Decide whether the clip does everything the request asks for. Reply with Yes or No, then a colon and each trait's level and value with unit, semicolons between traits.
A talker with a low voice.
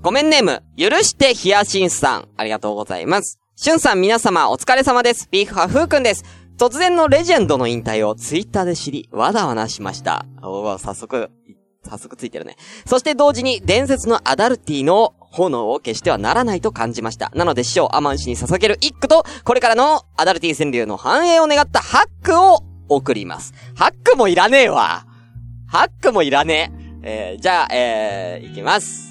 No: medium, 185 Hz